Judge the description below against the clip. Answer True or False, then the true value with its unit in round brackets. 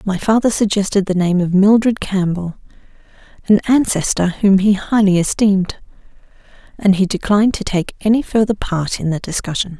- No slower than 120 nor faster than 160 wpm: True (155 wpm)